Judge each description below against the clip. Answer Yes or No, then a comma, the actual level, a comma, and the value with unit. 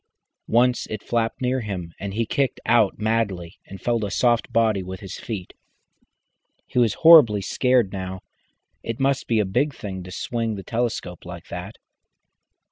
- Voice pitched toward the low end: Yes, low, 110 Hz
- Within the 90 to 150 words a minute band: No, average, 165 wpm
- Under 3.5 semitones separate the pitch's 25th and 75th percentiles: No, average, 3.8 semitones